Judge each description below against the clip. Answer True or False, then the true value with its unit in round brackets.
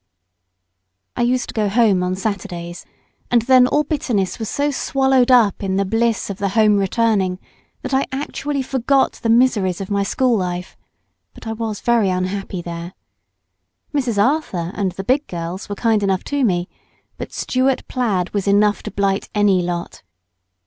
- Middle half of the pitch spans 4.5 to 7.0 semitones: True (4.8 semitones)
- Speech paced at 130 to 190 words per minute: True (165 wpm)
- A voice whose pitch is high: True (210 Hz)